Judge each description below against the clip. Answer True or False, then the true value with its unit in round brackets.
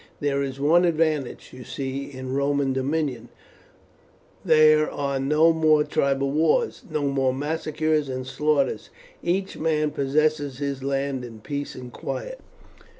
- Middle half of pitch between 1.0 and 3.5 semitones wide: True (2.4 semitones)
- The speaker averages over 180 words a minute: False (135 wpm)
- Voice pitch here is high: False (140 Hz)